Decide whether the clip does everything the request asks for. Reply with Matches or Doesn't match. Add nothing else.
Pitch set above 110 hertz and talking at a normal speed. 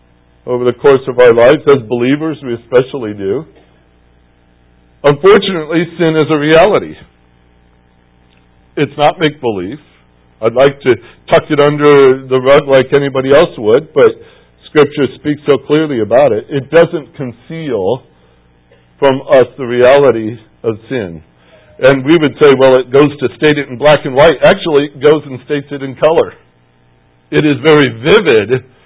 Matches